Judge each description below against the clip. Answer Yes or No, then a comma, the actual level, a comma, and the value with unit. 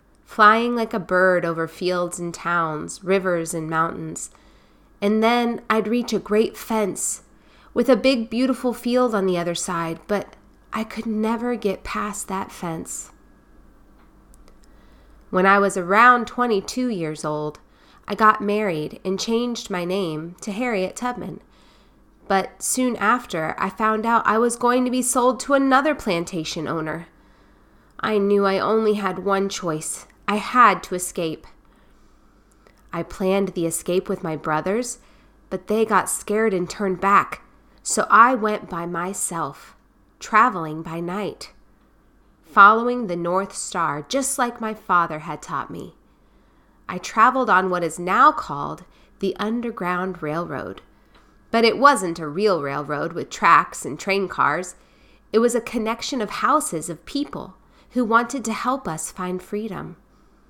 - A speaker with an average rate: Yes, average, 150 wpm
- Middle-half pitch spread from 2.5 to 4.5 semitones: No, average, 5.0 semitones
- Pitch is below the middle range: No, high, 200 Hz